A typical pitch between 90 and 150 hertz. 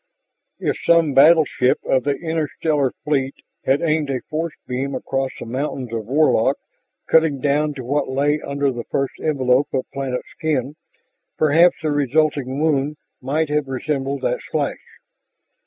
Yes: medium, 140 Hz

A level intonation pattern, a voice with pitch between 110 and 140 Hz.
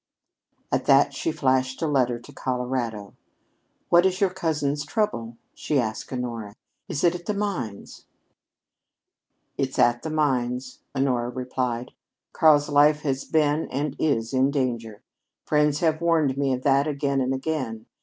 No: average, 3.6 semitones; low, 135 Hz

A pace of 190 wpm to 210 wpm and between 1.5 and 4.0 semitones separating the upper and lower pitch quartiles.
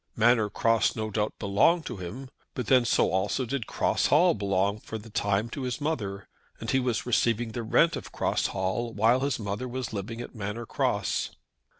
Yes: average, 195 wpm; average, 3.5 semitones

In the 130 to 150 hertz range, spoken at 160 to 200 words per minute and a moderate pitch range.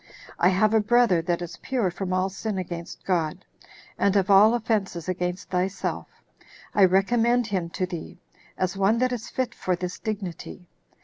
No: high, 190 Hz; average, 170 wpm; average, 3.3 semitones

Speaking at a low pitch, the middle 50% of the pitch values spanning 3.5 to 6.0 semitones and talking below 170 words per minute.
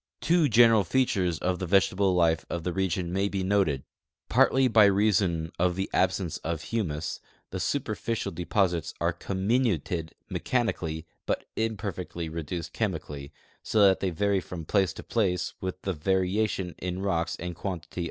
No: very low, 95 Hz; average, 3.1 semitones; average, 155 wpm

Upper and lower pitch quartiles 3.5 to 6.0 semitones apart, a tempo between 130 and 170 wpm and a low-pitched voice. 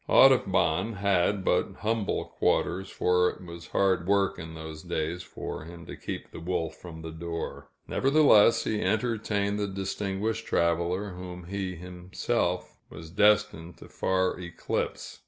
No: average, 3.1 semitones; average, 140 wpm; very low, 90 Hz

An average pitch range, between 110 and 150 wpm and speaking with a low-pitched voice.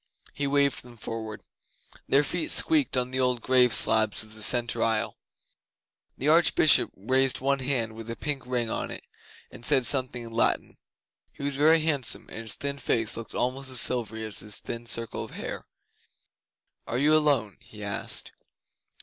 No: average, 3.6 semitones; average, 175 wpm; low, 125 Hz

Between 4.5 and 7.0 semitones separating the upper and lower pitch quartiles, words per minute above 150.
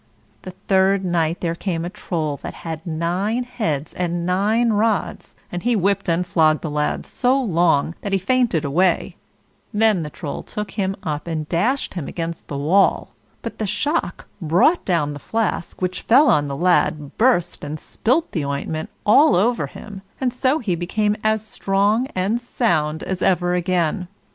Yes: average, 4.8 semitones; average, 175 wpm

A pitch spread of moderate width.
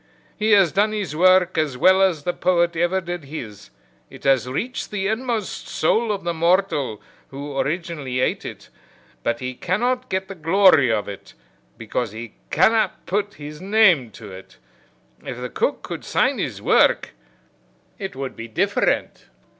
No: wide, 6.5 semitones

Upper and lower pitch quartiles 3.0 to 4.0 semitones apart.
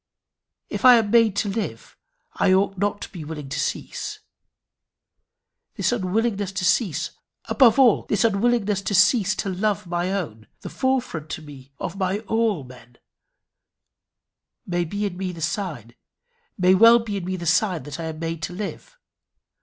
No: average, 4.4 semitones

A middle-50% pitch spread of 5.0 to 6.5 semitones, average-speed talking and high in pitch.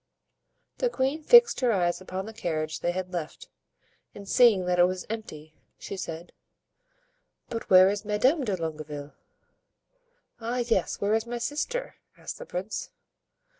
Yes: average, 5.3 semitones; average, 150 wpm; high, 200 Hz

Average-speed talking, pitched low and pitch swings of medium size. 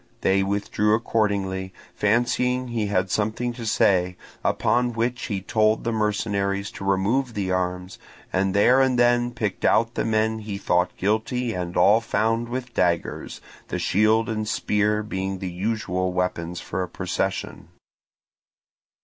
Yes: average, 145 wpm; low, 105 Hz; average, 3.3 semitones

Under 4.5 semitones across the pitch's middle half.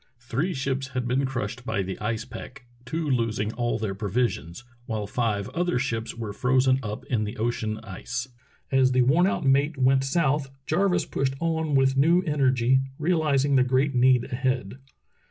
Yes: average, 3.0 semitones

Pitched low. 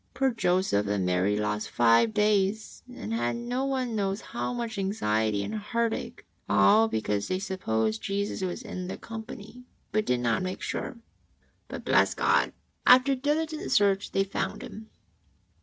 No: high, 200 Hz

